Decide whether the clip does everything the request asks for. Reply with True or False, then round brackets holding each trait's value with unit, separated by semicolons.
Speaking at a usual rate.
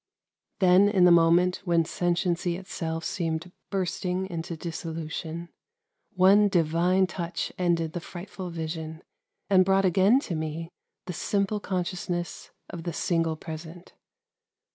False (120 wpm)